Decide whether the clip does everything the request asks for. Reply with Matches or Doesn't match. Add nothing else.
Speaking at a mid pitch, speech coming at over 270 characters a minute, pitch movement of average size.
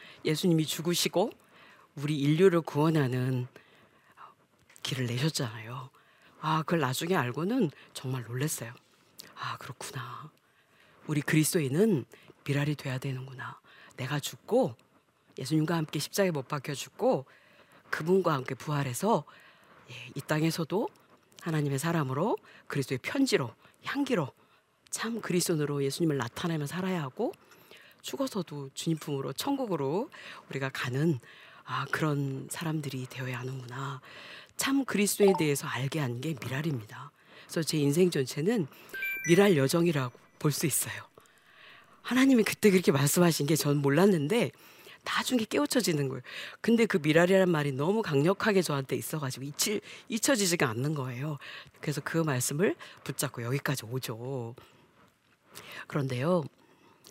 Matches